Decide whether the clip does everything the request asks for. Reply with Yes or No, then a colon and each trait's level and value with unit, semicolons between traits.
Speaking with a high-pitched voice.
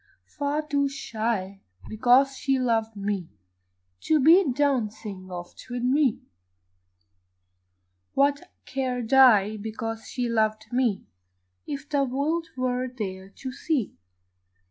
Yes: very high, 250 Hz